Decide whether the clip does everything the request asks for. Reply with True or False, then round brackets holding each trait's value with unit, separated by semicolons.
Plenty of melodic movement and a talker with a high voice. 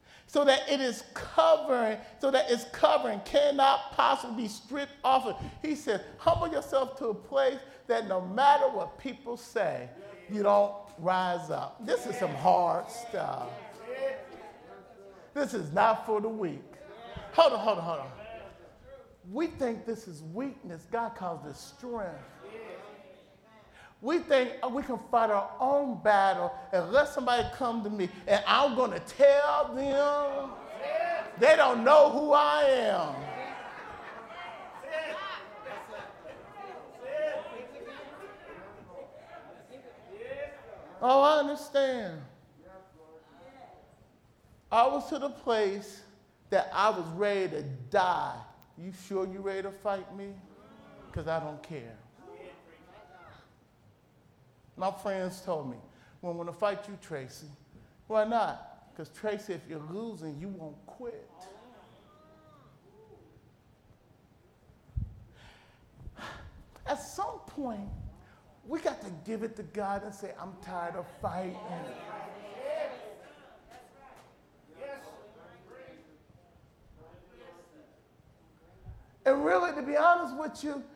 True (6.9 semitones; 230 Hz)